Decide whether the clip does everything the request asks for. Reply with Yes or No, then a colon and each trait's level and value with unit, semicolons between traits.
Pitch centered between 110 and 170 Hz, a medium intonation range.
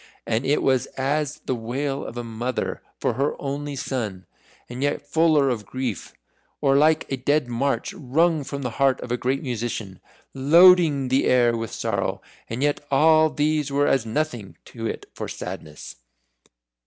Yes: low, 135 Hz; average, 3.4 semitones